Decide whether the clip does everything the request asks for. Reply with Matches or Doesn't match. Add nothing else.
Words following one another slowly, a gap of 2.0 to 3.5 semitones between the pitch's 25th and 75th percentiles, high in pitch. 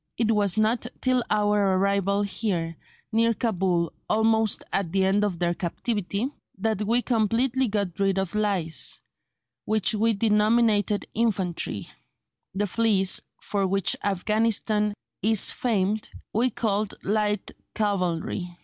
Matches